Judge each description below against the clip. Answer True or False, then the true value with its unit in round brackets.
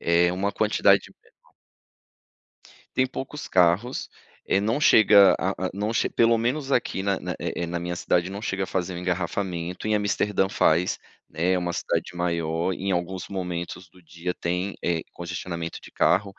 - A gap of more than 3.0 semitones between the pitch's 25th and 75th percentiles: False (2.7 semitones)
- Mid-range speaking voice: False (90 Hz)